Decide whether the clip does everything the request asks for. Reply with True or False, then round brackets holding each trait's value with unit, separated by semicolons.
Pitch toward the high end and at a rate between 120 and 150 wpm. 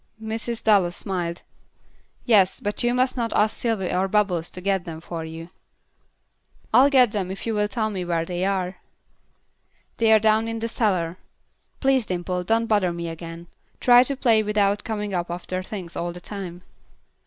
False (200 Hz; 175 wpm)